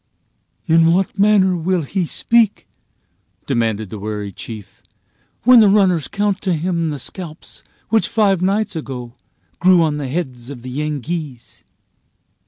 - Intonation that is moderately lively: No, wide, 6.8 semitones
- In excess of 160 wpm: No, average, 140 wpm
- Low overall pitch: No, medium, 165 Hz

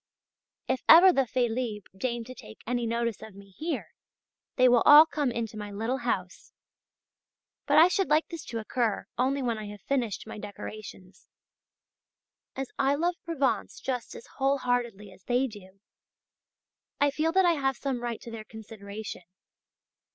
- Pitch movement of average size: Yes, average, 4.1 semitones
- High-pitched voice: Yes, high, 240 Hz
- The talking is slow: No, average, 165 wpm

